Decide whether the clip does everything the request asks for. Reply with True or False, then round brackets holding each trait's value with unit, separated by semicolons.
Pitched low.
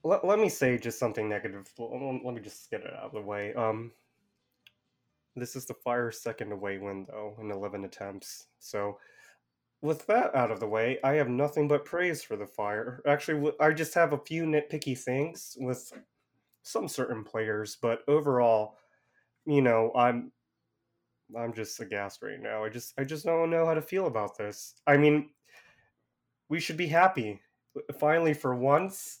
True (125 Hz)